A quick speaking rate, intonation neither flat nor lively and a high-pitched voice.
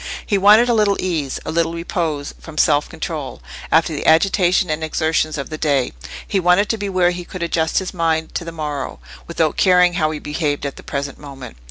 No: fast, 210 wpm; average, 3.1 semitones; medium, 160 Hz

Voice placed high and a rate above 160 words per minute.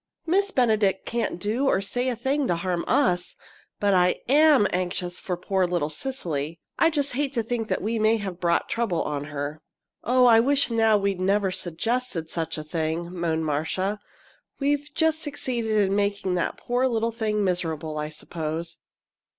Yes: high, 200 Hz; average, 170 wpm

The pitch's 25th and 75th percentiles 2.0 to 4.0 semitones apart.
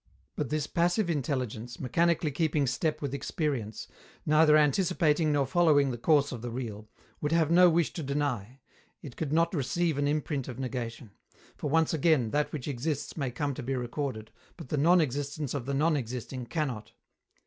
Yes: average, 3.7 semitones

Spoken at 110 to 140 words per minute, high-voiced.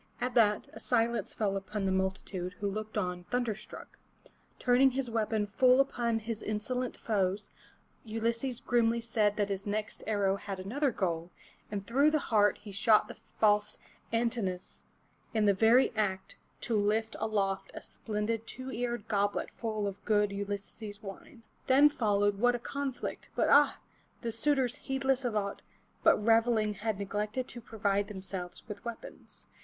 No: average, 160 wpm; high, 215 Hz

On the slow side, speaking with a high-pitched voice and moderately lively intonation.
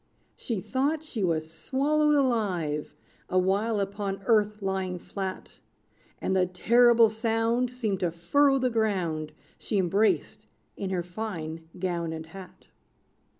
Yes: slow, 125 wpm; high, 195 Hz; average, 4.6 semitones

